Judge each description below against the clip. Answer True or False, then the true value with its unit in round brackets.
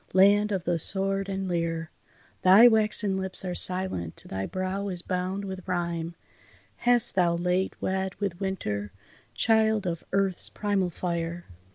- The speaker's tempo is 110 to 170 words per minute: True (145 wpm)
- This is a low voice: False (185 Hz)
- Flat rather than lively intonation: True (2.3 semitones)